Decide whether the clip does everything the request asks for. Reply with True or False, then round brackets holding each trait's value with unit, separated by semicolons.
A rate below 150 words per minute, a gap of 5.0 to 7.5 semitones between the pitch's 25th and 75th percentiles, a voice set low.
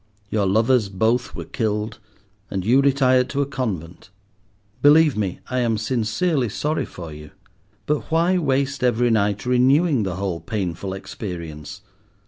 True (140 wpm; 5.6 semitones; 115 Hz)